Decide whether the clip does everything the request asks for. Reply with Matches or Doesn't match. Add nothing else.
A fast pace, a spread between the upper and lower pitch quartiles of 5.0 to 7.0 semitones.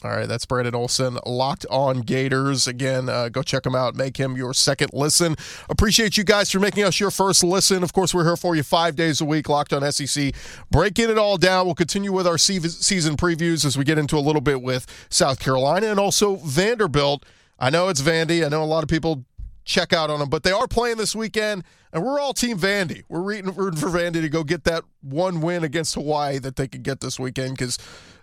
Matches